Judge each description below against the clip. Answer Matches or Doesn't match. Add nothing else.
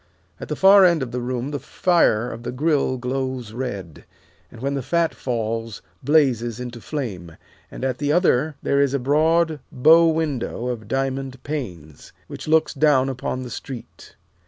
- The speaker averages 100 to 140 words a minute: Doesn't match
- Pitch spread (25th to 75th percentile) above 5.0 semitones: Doesn't match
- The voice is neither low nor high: Doesn't match